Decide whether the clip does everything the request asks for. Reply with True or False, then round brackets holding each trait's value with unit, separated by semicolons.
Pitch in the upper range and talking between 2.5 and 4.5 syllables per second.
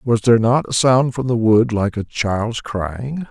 False (115 Hz; 4.0 syllables/s)